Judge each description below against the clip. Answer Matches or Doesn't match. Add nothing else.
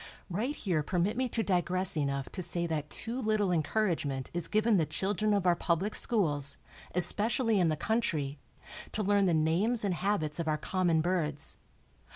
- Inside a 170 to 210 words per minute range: Matches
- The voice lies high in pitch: Doesn't match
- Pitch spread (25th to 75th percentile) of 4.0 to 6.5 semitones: Matches